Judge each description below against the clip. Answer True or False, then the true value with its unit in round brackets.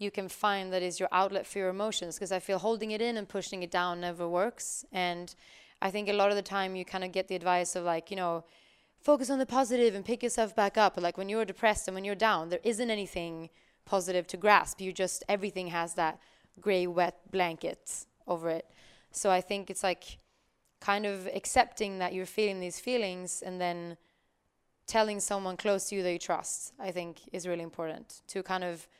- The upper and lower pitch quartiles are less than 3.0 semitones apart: True (2.5 semitones)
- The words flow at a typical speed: False (215 wpm)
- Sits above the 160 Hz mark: True (190 Hz)